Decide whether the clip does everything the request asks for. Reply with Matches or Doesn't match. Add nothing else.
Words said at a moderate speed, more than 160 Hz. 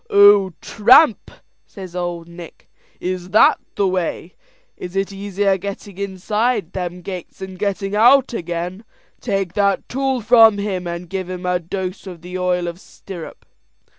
Matches